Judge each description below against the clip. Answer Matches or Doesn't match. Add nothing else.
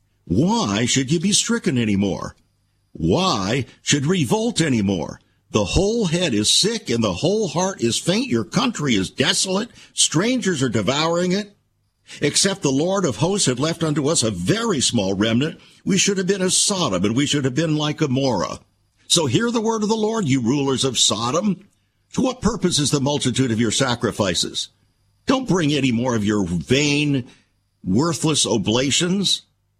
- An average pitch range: Doesn't match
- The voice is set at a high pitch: Doesn't match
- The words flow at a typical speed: Matches